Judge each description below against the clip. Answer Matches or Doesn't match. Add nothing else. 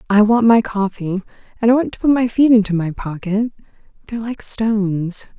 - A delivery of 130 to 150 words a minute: Doesn't match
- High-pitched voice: Matches